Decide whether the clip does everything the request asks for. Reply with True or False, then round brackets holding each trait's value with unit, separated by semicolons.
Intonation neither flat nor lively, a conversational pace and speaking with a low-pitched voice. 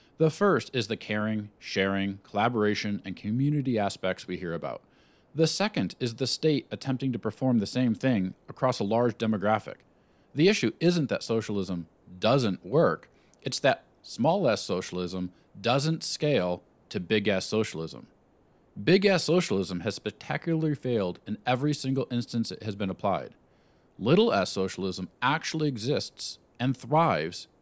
False (6.4 semitones; 145 wpm; 115 Hz)